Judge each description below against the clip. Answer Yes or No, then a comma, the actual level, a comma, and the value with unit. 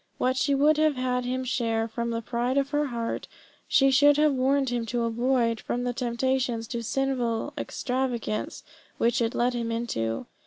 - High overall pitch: Yes, high, 245 Hz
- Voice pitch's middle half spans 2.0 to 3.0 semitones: Yes, narrow, 2.4 semitones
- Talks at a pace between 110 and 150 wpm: No, average, 180 wpm